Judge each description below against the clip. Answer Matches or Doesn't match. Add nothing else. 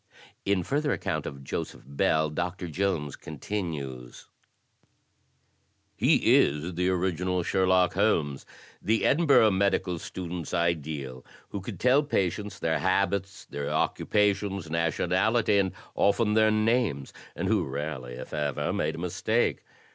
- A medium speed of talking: Doesn't match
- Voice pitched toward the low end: Matches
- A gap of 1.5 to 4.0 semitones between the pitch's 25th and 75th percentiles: Doesn't match